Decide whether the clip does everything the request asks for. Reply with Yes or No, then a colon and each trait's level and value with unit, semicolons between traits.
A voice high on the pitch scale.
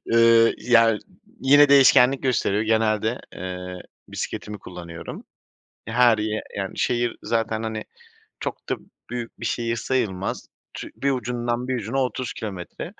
No: low, 115 Hz